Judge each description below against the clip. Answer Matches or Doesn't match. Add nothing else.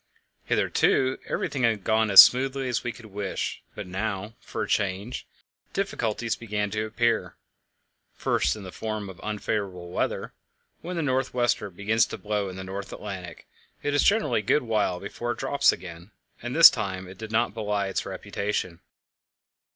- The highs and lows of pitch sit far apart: Doesn't match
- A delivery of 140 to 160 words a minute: Doesn't match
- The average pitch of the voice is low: Matches